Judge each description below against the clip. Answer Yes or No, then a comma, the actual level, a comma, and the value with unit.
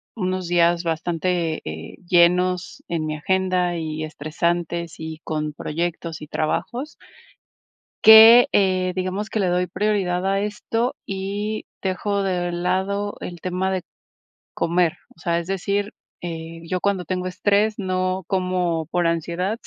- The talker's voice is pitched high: No, medium, 180 Hz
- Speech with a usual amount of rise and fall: No, narrow, 2.3 semitones